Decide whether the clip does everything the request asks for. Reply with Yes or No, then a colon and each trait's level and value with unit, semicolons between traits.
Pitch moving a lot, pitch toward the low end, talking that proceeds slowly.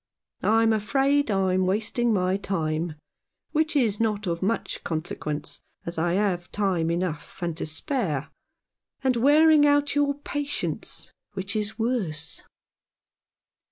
No: wide, 6.7 semitones; high, 205 Hz; slow, 125 wpm